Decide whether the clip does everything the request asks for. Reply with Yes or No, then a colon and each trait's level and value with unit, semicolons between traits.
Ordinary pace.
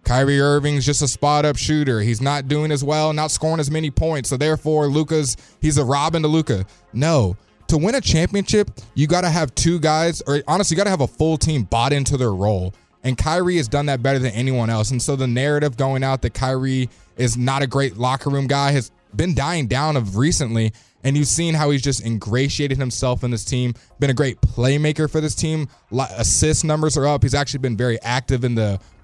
No: fast, 225 wpm